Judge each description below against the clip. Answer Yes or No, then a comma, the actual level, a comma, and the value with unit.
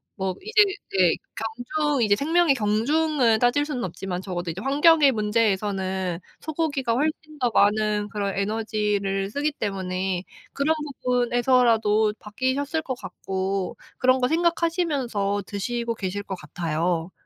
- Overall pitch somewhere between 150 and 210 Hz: No, high, 220 Hz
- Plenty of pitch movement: Yes, wide, 6.2 semitones